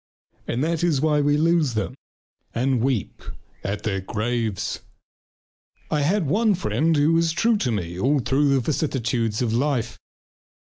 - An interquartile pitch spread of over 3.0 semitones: Yes, average, 5.3 semitones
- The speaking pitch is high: No, low, 135 Hz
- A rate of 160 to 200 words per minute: No, average, 150 wpm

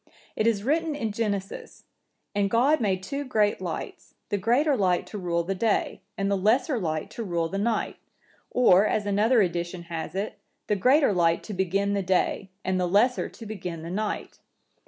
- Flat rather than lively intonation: No, average, 3.9 semitones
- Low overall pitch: No, high, 200 Hz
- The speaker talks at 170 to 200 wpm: Yes, average, 185 wpm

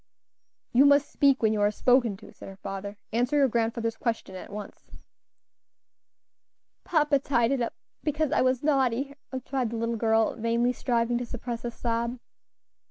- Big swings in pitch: No, average, 2.7 semitones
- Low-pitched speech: No, high, 235 Hz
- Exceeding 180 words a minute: No, average, 165 wpm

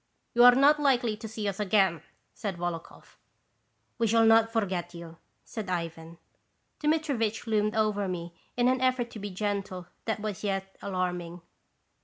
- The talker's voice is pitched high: Yes, high, 210 Hz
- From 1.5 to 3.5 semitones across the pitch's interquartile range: No, average, 3.9 semitones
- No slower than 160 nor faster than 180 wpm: Yes, average, 165 wpm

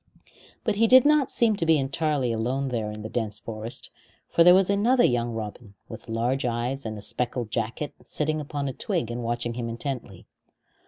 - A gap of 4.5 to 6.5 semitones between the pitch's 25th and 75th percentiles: Yes, average, 5.1 semitones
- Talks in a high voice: No, low, 125 Hz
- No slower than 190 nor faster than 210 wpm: Yes, average, 195 wpm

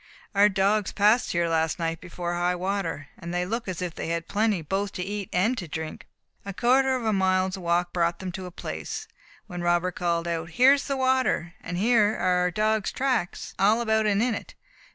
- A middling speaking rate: No, fast, 215 wpm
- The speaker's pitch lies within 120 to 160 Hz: No, high, 190 Hz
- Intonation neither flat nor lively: Yes, average, 3.8 semitones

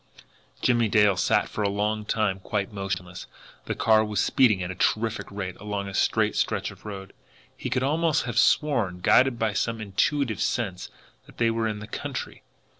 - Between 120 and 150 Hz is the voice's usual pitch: No, low, 105 Hz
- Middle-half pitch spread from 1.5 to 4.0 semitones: Yes, average, 2.7 semitones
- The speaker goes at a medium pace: Yes, average, 185 wpm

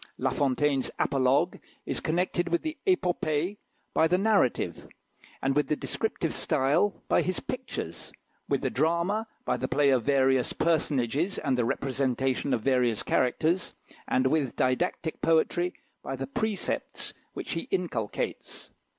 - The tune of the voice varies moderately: Yes, average, 4.8 semitones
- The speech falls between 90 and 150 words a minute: Yes, slow, 135 wpm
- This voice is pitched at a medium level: Yes, medium, 150 Hz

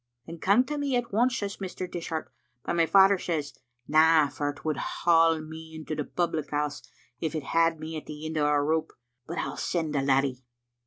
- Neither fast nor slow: No, fast, 220 wpm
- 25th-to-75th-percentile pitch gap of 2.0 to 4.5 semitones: Yes, average, 2.7 semitones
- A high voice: No, medium, 160 Hz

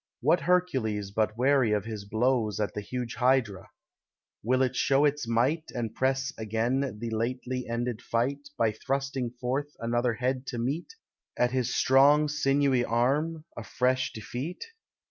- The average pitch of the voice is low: Yes, low, 125 Hz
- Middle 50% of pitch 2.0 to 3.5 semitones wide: Yes, average, 3.0 semitones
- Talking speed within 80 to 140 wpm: No, average, 150 wpm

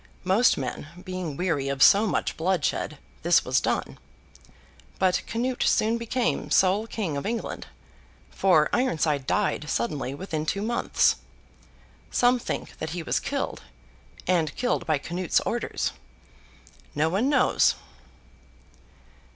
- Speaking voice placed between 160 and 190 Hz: Yes, medium, 185 Hz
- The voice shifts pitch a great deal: Yes, wide, 6.5 semitones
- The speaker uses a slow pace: Yes, slow, 125 wpm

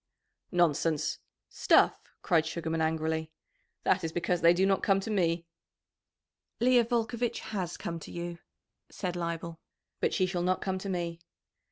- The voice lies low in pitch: No, medium, 175 Hz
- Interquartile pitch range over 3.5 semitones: No, narrow, 2.6 semitones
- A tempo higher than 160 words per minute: No, average, 150 wpm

